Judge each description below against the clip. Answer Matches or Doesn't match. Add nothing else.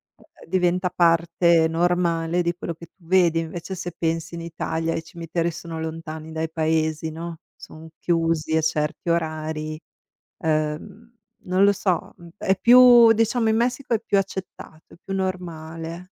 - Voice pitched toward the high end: Doesn't match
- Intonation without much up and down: Matches